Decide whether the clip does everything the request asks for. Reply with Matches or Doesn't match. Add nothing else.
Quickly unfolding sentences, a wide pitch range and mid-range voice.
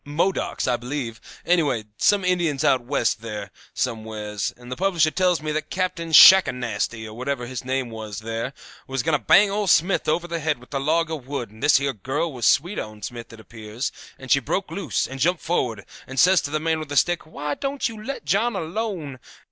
Matches